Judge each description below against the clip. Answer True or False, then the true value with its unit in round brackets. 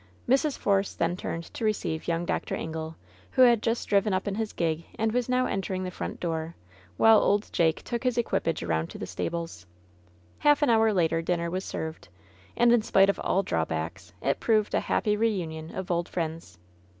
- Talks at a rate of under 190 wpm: False (195 wpm)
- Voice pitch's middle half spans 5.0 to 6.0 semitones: True (5.3 semitones)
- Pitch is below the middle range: False (185 Hz)